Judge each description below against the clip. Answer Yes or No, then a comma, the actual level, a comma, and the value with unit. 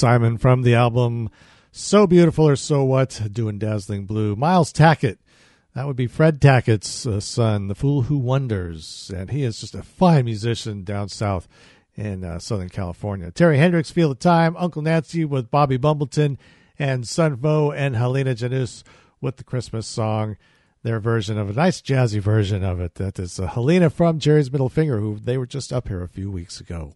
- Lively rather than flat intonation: Yes, wide, 5.7 semitones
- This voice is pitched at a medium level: No, low, 125 Hz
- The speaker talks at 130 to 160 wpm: No, average, 185 wpm